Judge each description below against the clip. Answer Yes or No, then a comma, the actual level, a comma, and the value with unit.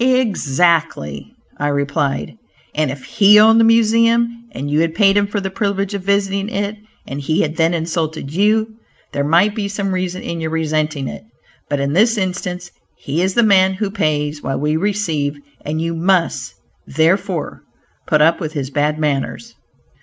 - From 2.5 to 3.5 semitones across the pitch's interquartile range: No, average, 5.1 semitones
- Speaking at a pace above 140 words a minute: Yes, average, 175 wpm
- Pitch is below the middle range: No, medium, 175 Hz